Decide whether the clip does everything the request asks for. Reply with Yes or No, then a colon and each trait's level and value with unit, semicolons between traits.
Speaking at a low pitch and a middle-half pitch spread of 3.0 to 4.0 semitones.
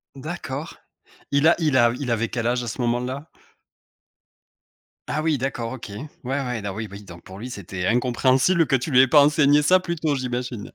Yes: low, 130 Hz; average, 3.7 semitones